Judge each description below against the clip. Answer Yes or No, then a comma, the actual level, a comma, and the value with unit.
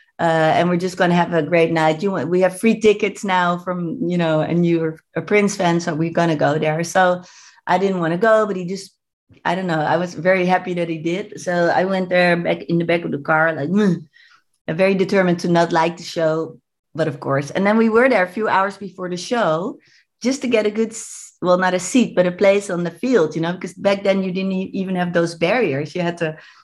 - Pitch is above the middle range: No, medium, 180 Hz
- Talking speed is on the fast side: Yes, fast, 255 wpm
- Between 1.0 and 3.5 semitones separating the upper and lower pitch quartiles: Yes, narrow, 2.6 semitones